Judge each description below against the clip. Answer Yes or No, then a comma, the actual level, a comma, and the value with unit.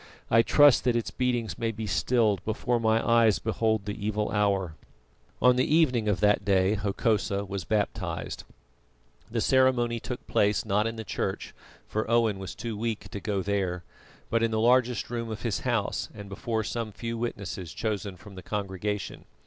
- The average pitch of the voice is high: No, low, 110 Hz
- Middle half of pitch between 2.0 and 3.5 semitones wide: Yes, narrow, 2.5 semitones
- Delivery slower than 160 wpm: No, average, 175 wpm